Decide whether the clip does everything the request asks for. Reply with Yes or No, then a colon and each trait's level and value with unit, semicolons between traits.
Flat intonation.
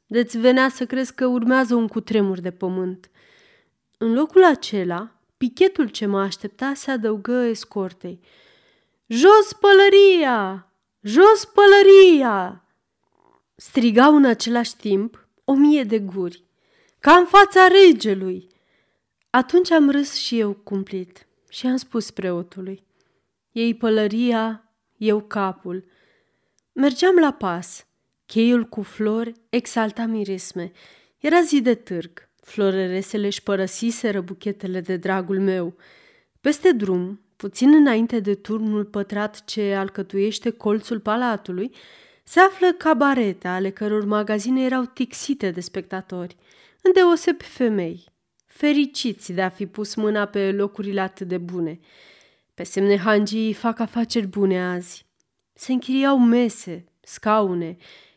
No: average, 5.3 semitones